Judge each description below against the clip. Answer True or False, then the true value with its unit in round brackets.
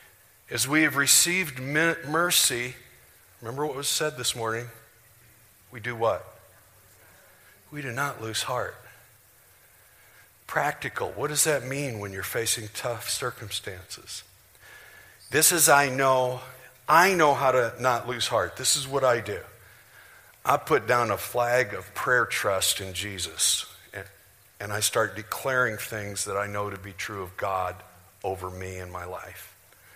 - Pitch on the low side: True (115 Hz)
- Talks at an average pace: True (150 wpm)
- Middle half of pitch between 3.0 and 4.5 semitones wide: False (5.0 semitones)